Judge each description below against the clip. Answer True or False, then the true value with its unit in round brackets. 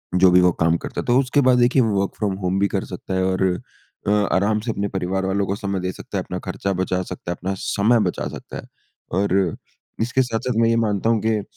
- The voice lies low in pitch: True (100 Hz)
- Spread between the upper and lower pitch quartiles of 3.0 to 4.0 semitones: True (3.3 semitones)